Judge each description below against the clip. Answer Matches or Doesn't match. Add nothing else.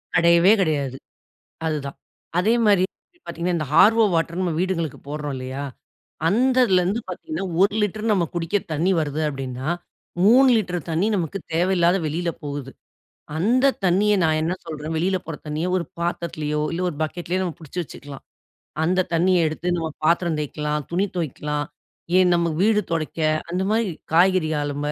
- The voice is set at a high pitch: Doesn't match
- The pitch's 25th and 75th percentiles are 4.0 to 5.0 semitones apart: Doesn't match